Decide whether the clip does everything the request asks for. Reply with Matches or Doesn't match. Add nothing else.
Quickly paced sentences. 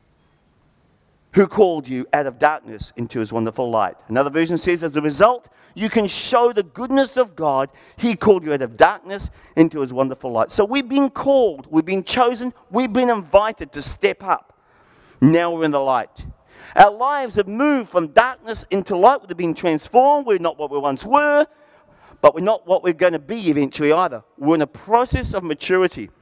Doesn't match